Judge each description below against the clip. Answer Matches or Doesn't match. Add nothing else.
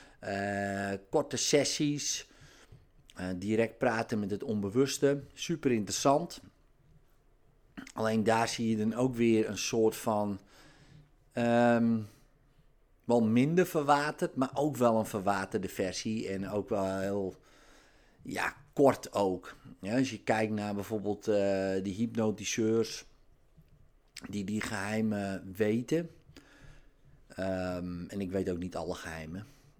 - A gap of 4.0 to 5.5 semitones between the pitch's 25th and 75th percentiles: Matches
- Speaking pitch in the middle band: Doesn't match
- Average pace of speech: Doesn't match